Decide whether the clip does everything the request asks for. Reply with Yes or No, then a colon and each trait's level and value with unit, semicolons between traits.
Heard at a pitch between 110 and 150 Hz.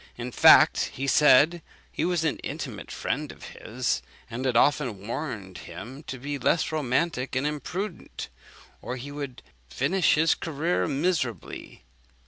Yes: medium, 140 Hz